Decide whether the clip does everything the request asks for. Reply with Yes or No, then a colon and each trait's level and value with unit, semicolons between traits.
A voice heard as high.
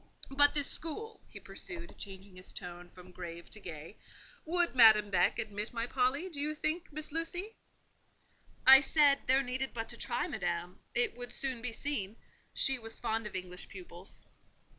Yes: high, 245 Hz